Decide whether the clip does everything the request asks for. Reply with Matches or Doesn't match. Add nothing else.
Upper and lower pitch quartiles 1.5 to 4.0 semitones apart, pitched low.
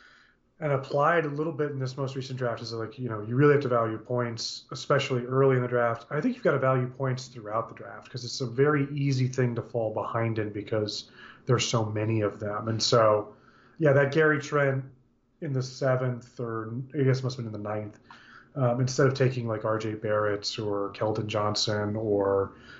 Matches